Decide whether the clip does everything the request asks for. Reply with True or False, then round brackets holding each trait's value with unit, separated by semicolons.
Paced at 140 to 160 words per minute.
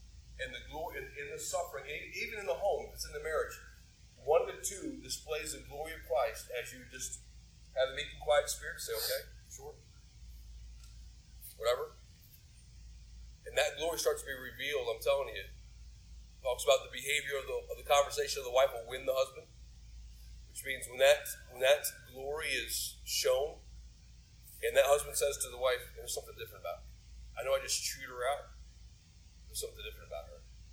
False (185 wpm)